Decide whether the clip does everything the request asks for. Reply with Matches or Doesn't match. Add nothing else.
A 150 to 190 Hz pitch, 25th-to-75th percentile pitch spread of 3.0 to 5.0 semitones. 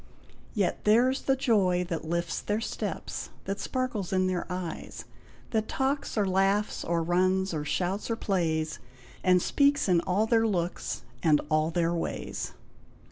Matches